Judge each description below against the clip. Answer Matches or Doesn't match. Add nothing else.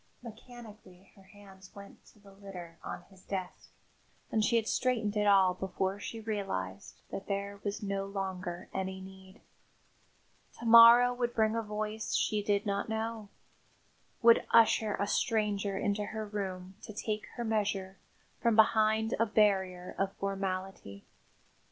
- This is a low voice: Doesn't match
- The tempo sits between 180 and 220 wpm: Doesn't match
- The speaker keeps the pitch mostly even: Matches